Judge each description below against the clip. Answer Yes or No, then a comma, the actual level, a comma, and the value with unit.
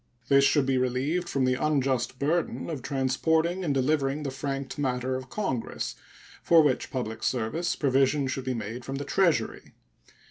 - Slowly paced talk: No, average, 165 wpm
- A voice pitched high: No, low, 135 Hz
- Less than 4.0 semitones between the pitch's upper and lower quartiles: Yes, average, 2.8 semitones